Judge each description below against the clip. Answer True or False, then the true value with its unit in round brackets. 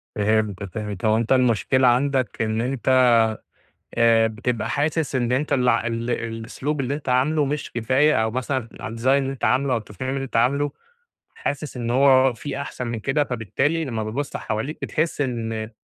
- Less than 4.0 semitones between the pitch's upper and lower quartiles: True (3.4 semitones)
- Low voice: True (125 Hz)